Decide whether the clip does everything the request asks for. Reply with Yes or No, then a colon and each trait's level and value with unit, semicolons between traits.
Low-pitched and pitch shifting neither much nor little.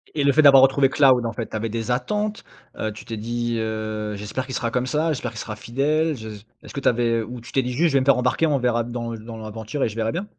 Yes: low, 120 Hz; average, 3.5 semitones